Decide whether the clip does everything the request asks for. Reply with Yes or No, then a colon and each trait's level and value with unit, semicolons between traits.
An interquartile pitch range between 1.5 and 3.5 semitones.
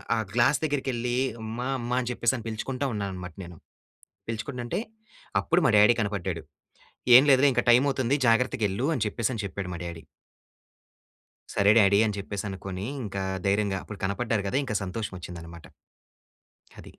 No: average, 3.9 semitones